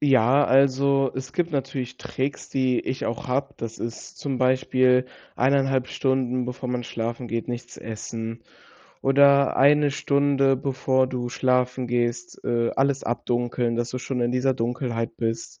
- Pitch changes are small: Yes, narrow, 2.1 semitones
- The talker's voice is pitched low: Yes, low, 130 Hz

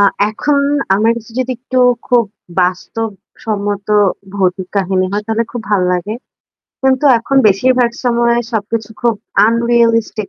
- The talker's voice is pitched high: Yes, high, 225 Hz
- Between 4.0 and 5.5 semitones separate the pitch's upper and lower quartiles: No, average, 2.9 semitones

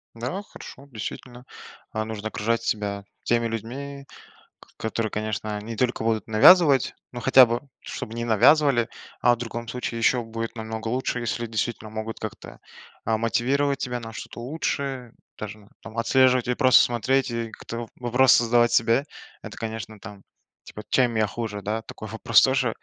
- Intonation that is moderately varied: No, narrow, 2.3 semitones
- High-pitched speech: No, low, 115 Hz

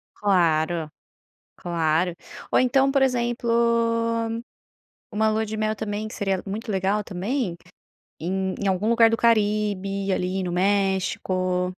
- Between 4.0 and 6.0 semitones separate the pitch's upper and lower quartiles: No, average, 3.0 semitones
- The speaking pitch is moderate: No, high, 200 Hz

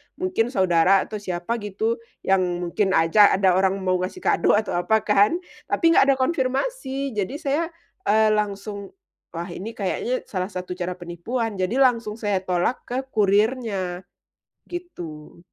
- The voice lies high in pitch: Yes, high, 210 Hz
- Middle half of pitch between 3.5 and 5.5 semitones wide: Yes, average, 5.1 semitones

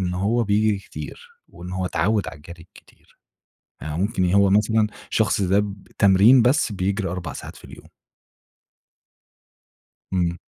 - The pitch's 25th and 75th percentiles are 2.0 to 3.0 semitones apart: Yes, average, 2.7 semitones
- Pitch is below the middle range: Yes, low, 100 Hz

